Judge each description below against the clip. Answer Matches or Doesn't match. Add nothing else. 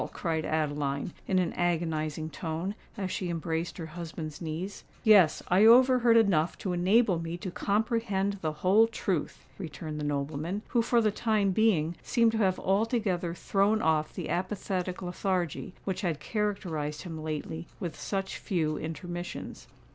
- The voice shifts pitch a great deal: Doesn't match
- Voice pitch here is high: Doesn't match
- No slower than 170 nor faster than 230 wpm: Doesn't match